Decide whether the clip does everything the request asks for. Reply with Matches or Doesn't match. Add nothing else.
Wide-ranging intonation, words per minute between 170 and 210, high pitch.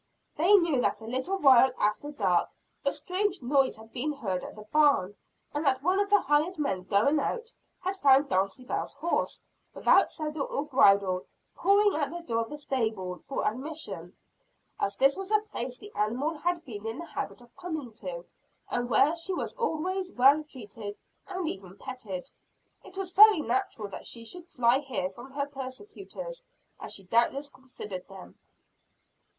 Matches